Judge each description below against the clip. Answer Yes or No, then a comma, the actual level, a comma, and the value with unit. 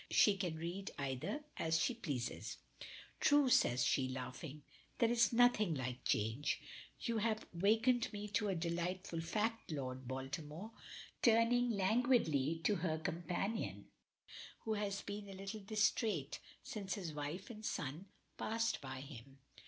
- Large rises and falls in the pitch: Yes, wide, 6.9 semitones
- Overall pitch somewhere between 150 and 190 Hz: Yes, medium, 185 Hz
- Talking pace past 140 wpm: No, slow, 135 wpm